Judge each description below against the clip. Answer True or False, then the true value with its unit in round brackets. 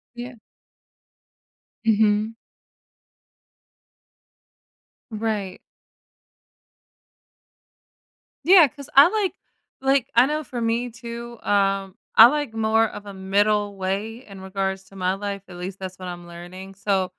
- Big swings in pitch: False (3.7 semitones)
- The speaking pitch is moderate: False (210 Hz)